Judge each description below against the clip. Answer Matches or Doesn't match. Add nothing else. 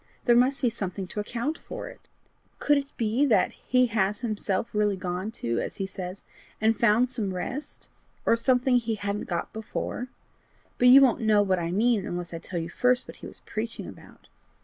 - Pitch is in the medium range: Doesn't match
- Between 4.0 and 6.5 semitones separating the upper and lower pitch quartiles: Matches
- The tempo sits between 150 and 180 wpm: Doesn't match